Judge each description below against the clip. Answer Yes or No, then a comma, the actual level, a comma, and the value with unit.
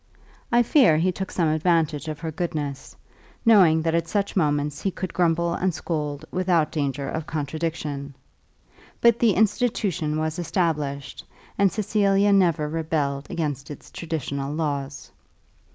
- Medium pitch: Yes, medium, 160 Hz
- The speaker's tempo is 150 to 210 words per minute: No, slow, 135 wpm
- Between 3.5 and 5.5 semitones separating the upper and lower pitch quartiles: Yes, average, 3.8 semitones